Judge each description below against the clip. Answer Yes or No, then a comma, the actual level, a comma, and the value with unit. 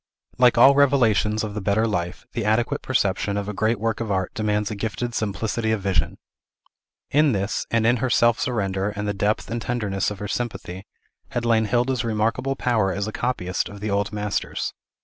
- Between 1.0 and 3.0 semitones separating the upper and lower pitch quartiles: Yes, average, 2.7 semitones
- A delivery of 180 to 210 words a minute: Yes, average, 195 wpm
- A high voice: No, low, 110 Hz